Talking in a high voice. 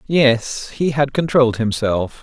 No: low, 130 Hz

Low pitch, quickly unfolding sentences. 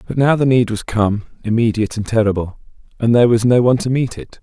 Yes: low, 115 Hz; fast, 230 wpm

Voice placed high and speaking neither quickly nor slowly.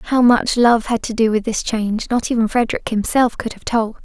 No: high, 230 Hz; fast, 240 wpm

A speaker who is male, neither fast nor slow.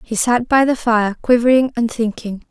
No: female; average, 190 wpm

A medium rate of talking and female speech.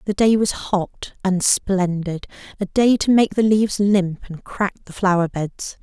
Yes: average, 185 wpm; female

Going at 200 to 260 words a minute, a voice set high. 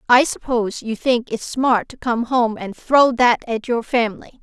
Yes: fast, 205 wpm; high, 240 Hz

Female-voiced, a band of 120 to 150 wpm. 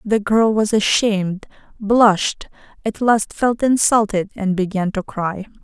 Yes: female; average, 140 wpm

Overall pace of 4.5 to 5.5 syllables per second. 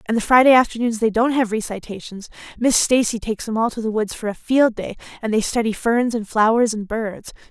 No: 5.7 syllables/s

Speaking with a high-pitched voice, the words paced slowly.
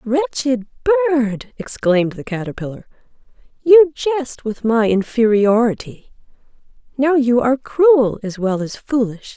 Yes: high, 240 Hz; slow, 110 wpm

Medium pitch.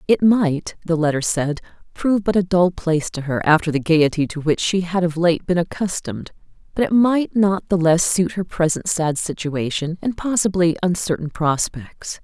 Yes: medium, 175 Hz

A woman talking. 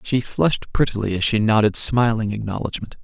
No: male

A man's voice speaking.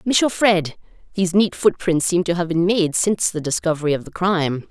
No: female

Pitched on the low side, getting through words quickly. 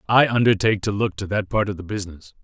Yes: low, 105 Hz; fast, 245 wpm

